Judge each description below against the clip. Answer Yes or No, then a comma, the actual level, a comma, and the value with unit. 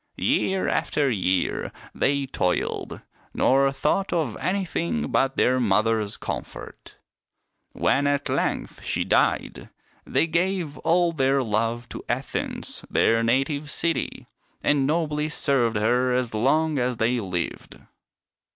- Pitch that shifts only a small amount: No, average, 4.9 semitones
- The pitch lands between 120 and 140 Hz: Yes, low, 135 Hz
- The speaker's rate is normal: No, slow, 120 wpm